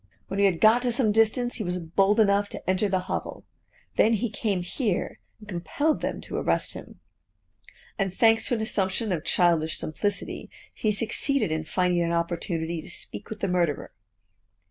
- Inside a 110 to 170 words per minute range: No, average, 180 wpm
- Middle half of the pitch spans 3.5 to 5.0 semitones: Yes, average, 4.0 semitones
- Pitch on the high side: Yes, high, 195 Hz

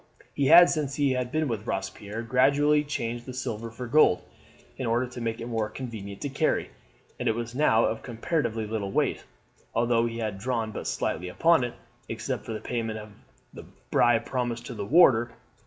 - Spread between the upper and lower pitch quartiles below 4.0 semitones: Yes, average, 2.8 semitones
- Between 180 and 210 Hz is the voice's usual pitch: No, low, 120 Hz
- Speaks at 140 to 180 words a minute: No, average, 190 wpm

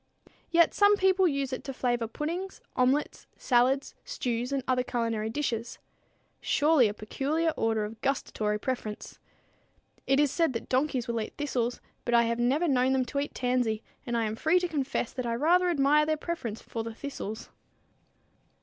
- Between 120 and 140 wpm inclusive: No, average, 175 wpm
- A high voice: Yes, very high, 255 Hz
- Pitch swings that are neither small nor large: Yes, average, 4.4 semitones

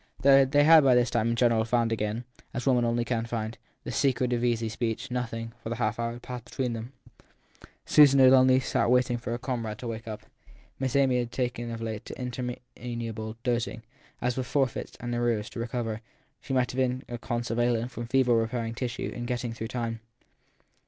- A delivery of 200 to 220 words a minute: Yes, fast, 205 wpm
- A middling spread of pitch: No, narrow, 1.6 semitones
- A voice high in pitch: No, low, 120 Hz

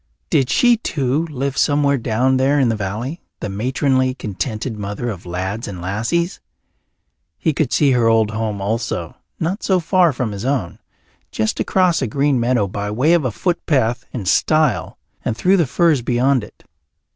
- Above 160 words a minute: Yes, average, 170 wpm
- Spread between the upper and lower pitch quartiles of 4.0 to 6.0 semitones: Yes, average, 5.2 semitones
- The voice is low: Yes, low, 125 Hz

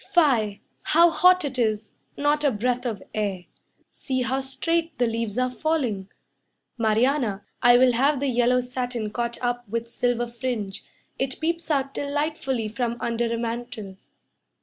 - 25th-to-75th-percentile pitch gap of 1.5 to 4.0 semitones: Yes, average, 3.1 semitones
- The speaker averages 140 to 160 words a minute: Yes, average, 150 wpm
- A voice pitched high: Yes, high, 245 Hz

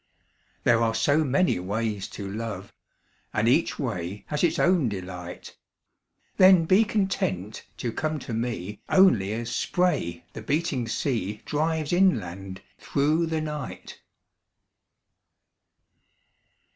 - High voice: No, low, 120 Hz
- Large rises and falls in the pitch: Yes, wide, 8.2 semitones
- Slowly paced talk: Yes, slow, 115 wpm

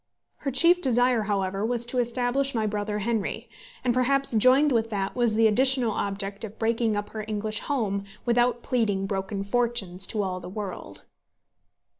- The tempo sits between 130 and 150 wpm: No, average, 165 wpm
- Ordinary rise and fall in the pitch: Yes, average, 3.3 semitones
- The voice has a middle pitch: No, high, 225 Hz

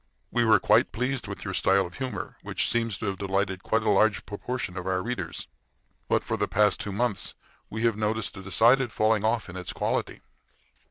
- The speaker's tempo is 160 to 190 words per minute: No, fast, 205 wpm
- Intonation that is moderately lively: Yes, average, 3.1 semitones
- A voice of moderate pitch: No, low, 105 Hz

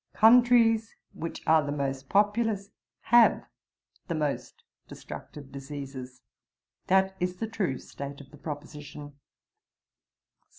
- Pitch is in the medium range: Yes, medium, 155 Hz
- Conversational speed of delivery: No, slow, 110 wpm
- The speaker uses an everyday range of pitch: No, wide, 6.8 semitones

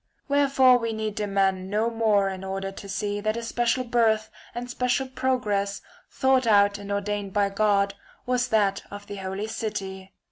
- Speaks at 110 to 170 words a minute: No, average, 185 wpm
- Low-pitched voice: No, high, 210 Hz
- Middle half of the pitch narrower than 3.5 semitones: Yes, average, 2.9 semitones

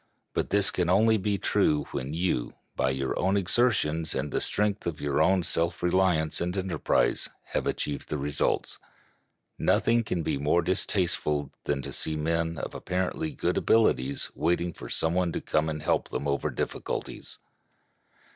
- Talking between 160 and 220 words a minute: Yes, average, 165 wpm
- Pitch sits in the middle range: No, very low, 85 Hz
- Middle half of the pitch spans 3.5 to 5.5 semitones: Yes, average, 4.0 semitones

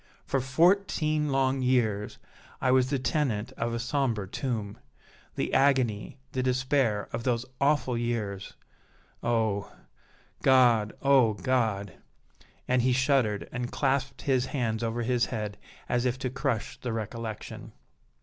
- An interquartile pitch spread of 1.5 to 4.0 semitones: Yes, average, 3.0 semitones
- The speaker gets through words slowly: Yes, slow, 130 wpm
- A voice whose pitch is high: No, low, 125 Hz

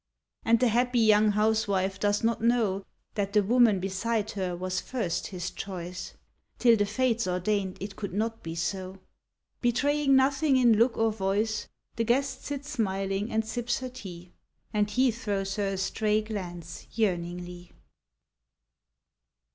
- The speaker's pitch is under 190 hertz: No, high, 210 Hz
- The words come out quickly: No, average, 145 wpm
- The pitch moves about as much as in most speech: Yes, average, 3.4 semitones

